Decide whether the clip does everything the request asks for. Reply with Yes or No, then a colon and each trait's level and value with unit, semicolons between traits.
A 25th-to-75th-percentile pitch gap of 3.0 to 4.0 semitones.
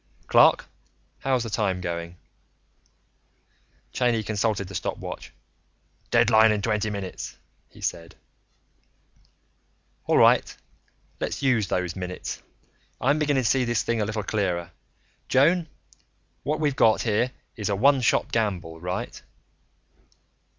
No: average, 4.9 semitones